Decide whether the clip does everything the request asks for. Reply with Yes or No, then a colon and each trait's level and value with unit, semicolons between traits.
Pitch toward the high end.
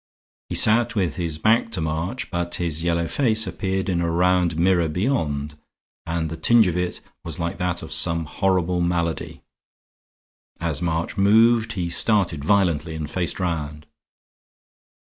No: very low, 85 Hz